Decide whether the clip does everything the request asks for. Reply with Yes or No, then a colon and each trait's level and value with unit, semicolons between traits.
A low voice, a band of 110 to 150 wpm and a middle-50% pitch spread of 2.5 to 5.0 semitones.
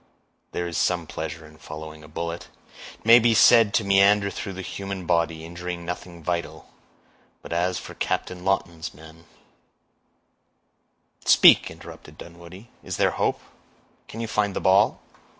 Yes: very low, 90 Hz; average, 145 wpm; average, 3.0 semitones